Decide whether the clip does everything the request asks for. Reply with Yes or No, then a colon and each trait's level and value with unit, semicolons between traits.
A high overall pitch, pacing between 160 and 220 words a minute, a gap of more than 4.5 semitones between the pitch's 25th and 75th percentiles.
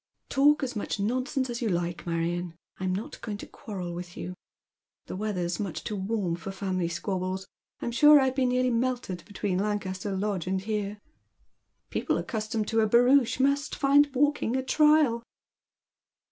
Yes: high, 210 Hz; average, 170 wpm; average, 5.3 semitones